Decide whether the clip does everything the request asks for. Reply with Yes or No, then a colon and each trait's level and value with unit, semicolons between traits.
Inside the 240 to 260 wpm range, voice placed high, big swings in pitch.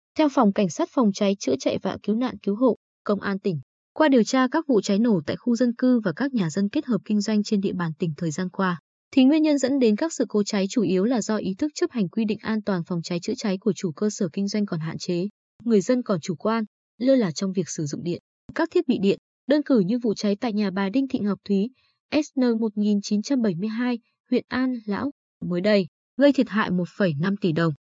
No: fast, 250 wpm; high, 210 Hz; average, 4.3 semitones